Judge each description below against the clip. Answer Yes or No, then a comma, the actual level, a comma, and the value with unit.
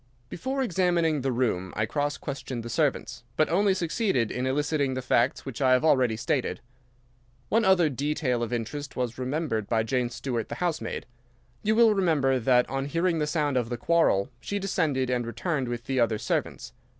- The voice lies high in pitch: No, low, 135 Hz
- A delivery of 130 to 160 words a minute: No, average, 185 wpm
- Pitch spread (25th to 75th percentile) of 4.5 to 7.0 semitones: Yes, average, 5.1 semitones